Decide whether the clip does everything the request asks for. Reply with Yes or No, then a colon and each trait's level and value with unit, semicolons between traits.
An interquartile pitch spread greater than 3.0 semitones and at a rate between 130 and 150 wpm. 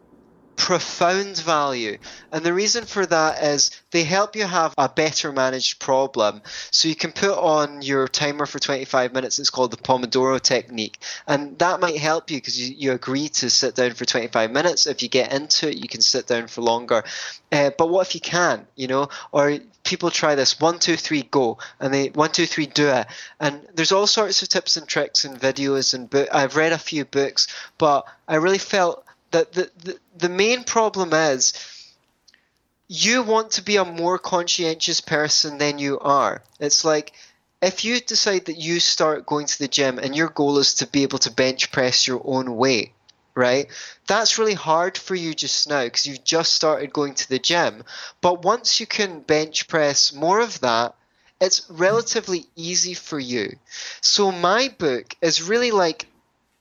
No: average, 4.5 semitones; average, 190 wpm